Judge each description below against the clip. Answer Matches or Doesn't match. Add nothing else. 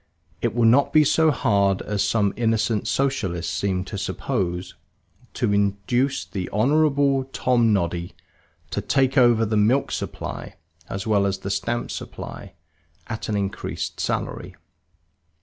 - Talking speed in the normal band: Doesn't match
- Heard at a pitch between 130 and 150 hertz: Doesn't match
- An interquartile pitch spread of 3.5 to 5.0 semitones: Matches